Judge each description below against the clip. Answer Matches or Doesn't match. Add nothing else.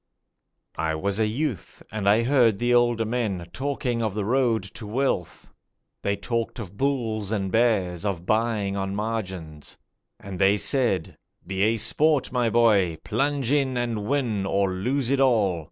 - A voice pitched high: Doesn't match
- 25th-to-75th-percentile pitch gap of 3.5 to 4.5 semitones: Matches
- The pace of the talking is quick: Doesn't match